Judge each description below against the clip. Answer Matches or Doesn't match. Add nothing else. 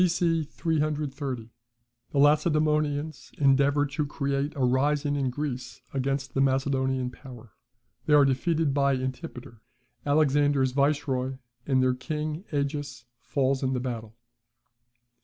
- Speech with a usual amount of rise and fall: Doesn't match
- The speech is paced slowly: Matches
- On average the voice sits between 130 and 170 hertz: Matches